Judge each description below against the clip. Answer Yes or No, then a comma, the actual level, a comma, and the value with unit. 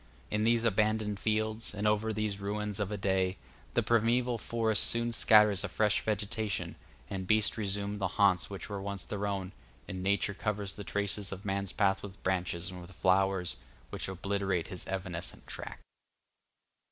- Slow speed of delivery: No, average, 165 wpm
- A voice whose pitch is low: Yes, low, 100 Hz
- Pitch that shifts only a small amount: Yes, narrow, 1.9 semitones